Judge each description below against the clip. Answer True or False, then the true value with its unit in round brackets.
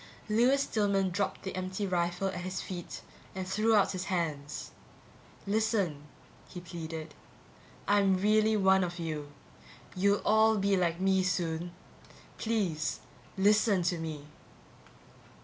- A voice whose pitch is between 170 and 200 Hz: True (185 Hz)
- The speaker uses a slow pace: True (125 wpm)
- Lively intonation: False (3.0 semitones)